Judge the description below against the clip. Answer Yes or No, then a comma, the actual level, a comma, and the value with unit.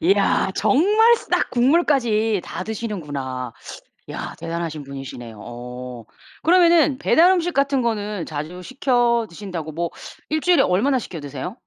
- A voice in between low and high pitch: No, high, 205 Hz